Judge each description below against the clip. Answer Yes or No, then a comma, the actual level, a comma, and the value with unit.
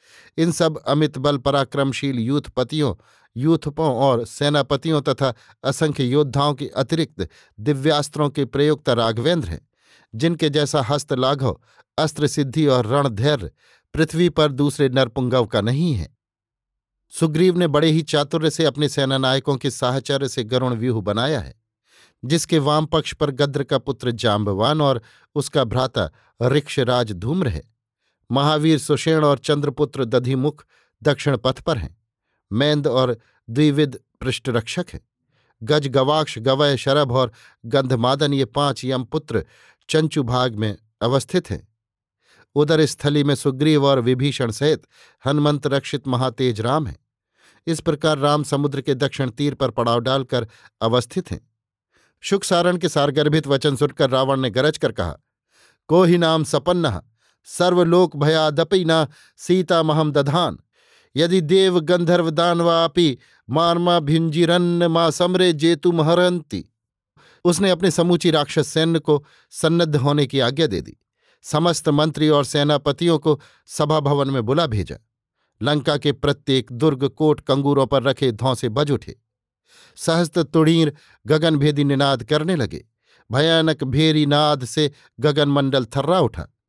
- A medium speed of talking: Yes, average, 130 wpm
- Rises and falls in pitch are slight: No, average, 3.3 semitones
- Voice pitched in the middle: Yes, medium, 145 Hz